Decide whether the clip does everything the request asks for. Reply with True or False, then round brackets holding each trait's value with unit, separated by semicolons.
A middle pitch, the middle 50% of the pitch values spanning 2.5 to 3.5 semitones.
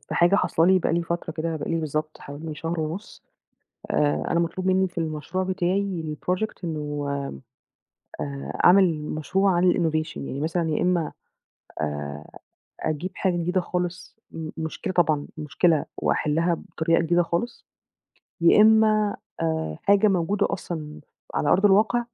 True (170 Hz; 3.0 semitones)